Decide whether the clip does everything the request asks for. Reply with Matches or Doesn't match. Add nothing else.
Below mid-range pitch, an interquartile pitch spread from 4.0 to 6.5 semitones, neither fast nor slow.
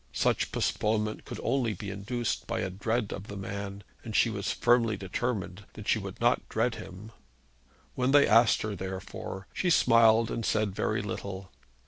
Doesn't match